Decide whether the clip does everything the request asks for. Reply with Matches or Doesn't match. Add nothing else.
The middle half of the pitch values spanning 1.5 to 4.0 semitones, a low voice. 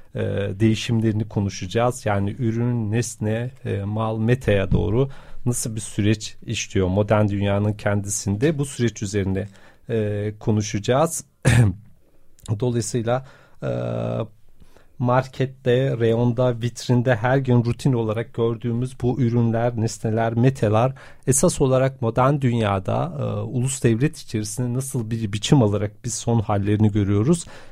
Matches